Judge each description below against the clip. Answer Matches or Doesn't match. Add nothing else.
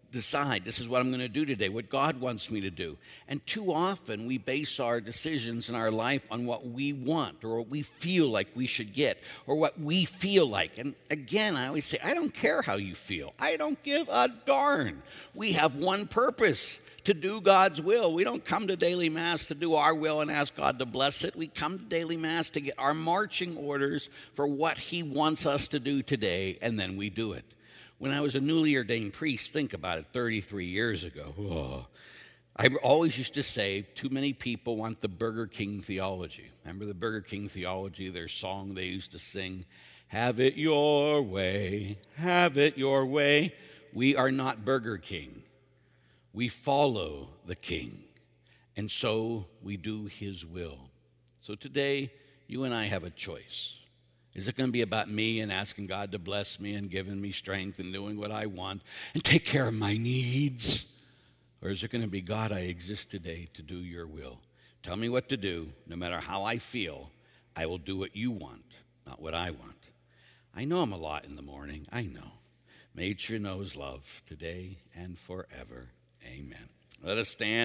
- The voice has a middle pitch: Doesn't match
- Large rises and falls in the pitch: Matches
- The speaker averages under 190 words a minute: Doesn't match